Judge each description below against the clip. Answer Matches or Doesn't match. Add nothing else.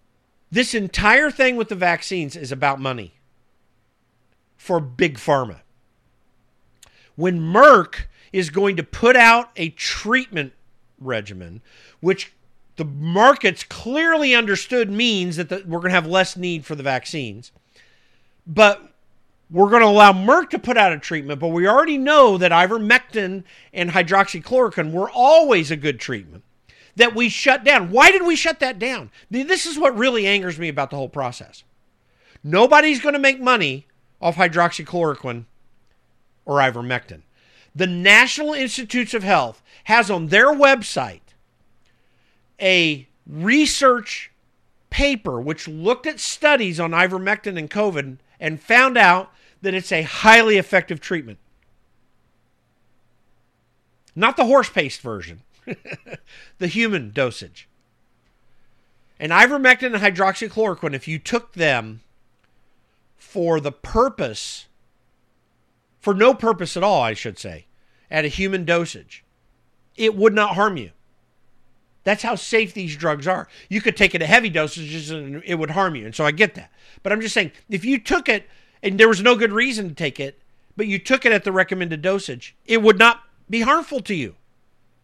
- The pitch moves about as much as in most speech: Doesn't match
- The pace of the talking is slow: Doesn't match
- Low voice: Doesn't match